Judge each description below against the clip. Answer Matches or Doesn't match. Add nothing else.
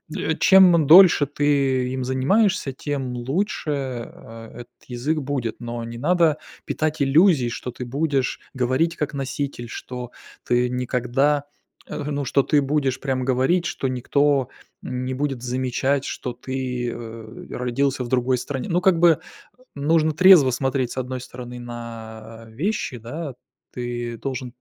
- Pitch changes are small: Doesn't match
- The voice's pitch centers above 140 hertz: Doesn't match